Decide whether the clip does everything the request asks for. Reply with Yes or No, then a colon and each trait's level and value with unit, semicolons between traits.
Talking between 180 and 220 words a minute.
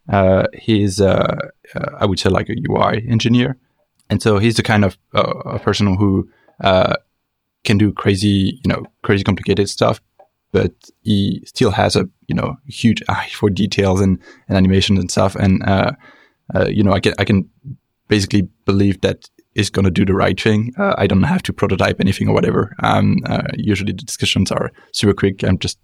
Yes: average, 195 wpm